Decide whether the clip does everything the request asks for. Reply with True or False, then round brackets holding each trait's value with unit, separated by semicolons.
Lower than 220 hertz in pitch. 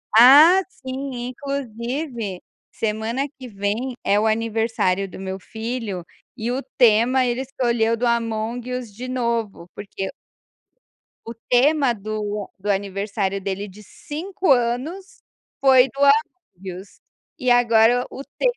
False (235 Hz)